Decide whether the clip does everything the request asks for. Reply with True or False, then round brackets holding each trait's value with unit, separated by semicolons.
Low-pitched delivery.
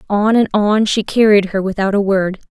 False (205 Hz)